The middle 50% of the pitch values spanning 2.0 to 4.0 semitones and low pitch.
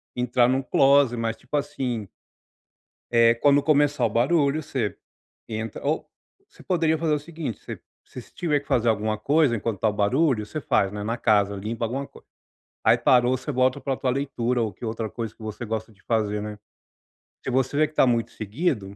No: average, 4.4 semitones; low, 120 Hz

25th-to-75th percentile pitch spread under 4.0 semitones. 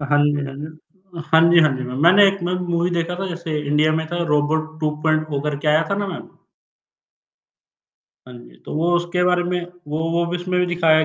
Yes: narrow, 2.6 semitones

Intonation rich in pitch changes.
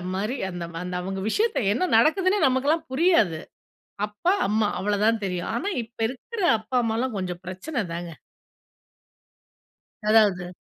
Yes: wide, 6.9 semitones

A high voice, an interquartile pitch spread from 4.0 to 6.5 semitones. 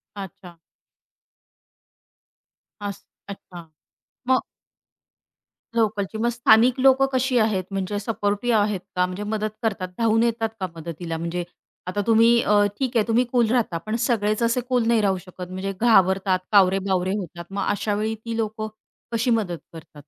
No: high, 210 Hz; average, 3.4 semitones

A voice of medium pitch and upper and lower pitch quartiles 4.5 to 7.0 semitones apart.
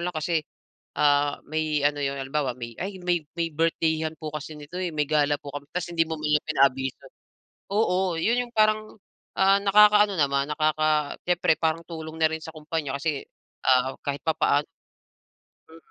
No: medium, 155 Hz; average, 2.9 semitones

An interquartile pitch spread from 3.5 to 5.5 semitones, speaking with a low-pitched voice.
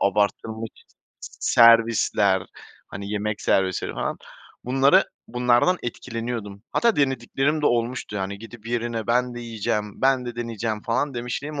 No: average, 2.7 semitones; low, 115 Hz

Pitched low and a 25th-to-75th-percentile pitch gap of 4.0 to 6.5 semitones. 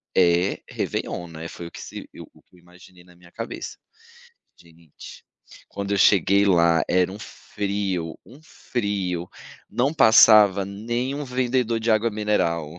Yes: low, 100 Hz; average, 4.3 semitones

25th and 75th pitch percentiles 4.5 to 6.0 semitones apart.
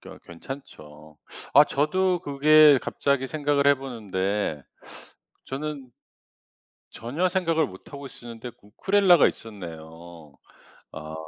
No: wide, 8.3 semitones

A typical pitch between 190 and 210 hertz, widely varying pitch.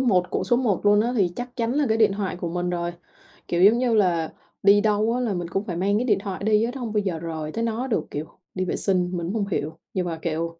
No: high, 200 Hz; average, 4.2 semitones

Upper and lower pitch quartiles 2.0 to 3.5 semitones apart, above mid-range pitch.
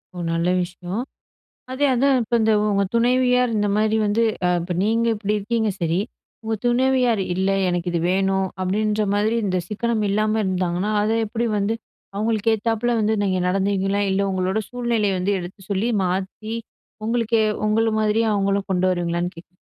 Yes: average, 3.2 semitones; high, 210 Hz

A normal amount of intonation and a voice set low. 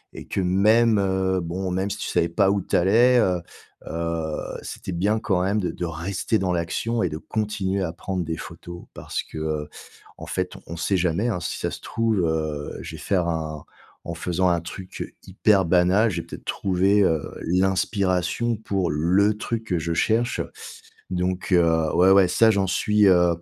Yes: average, 3.0 semitones; very low, 95 Hz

